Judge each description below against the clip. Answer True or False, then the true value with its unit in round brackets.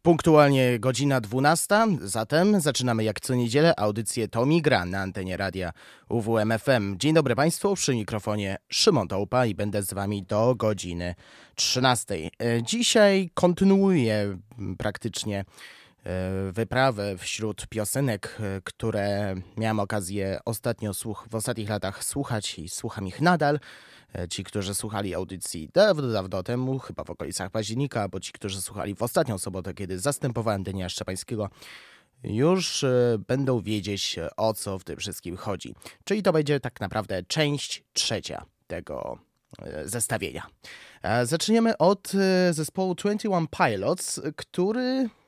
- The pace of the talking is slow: False (125 wpm)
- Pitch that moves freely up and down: True (6.5 semitones)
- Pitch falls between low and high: False (115 Hz)